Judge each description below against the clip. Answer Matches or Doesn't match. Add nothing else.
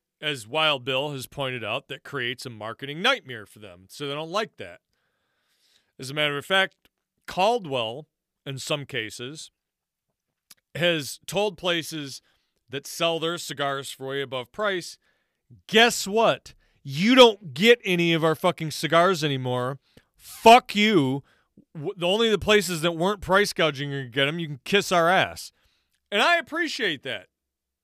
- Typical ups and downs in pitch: Doesn't match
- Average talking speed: Matches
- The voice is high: Doesn't match